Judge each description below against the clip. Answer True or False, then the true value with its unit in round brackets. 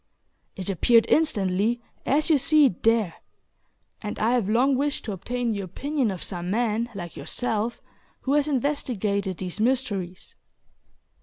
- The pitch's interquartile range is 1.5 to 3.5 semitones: False (5.1 semitones)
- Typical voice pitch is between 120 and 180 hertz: False (225 Hz)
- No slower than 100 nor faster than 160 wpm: True (145 wpm)